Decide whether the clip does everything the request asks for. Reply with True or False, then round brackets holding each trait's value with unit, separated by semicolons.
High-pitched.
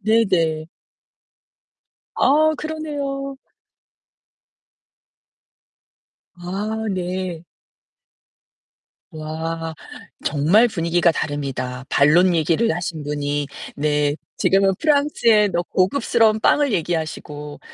False (175 Hz)